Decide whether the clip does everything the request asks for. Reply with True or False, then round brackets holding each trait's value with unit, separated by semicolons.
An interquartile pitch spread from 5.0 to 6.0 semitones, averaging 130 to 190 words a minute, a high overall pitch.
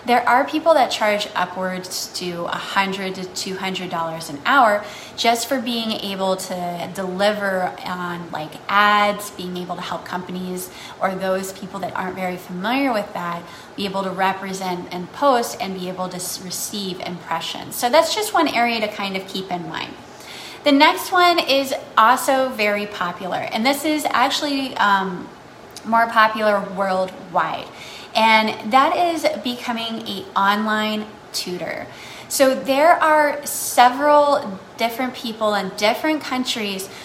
True (5.5 semitones; 145 wpm; 205 Hz)